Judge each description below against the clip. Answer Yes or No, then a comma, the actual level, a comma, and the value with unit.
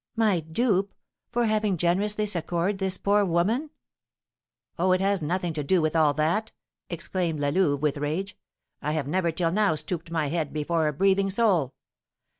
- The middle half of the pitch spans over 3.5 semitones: Yes, average, 4.1 semitones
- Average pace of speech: Yes, average, 170 wpm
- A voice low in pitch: No, medium, 175 Hz